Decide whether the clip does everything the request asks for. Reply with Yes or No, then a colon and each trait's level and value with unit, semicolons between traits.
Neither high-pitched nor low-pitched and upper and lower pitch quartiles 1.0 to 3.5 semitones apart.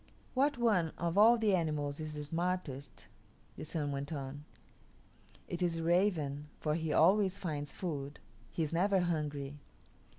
No: medium, 165 Hz; average, 3.9 semitones